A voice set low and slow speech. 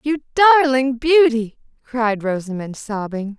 No: very high, 250 Hz; slow, 105 wpm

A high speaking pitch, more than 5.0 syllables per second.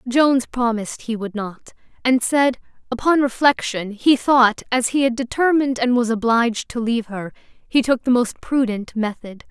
No: high, 240 Hz; 4.8 syllables/s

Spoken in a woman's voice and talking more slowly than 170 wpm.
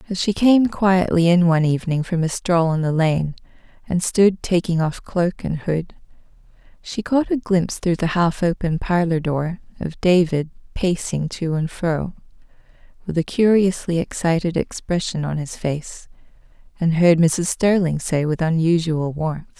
Yes: female; average, 160 wpm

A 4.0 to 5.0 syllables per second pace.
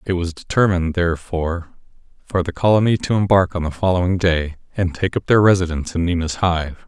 No: 6.0 syllables/s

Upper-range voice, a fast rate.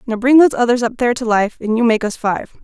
Yes: high, 235 Hz; fast, 295 wpm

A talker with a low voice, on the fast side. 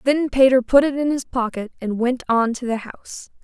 No: very high, 250 Hz; fast, 225 wpm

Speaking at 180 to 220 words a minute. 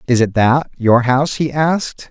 Yes: average, 200 wpm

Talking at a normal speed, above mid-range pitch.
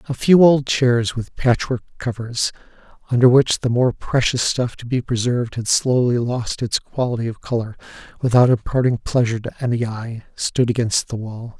No: average, 175 wpm; low, 120 Hz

